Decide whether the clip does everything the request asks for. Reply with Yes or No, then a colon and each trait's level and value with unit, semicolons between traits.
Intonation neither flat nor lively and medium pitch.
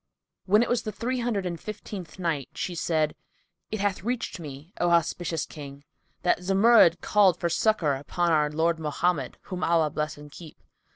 Yes: average, 4.7 semitones; medium, 170 Hz